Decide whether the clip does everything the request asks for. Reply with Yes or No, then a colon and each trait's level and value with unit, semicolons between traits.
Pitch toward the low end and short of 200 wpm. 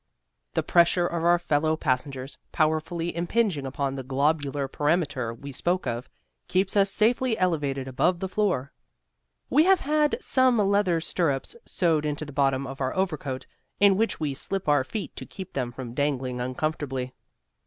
No: medium, 155 Hz; average, 160 wpm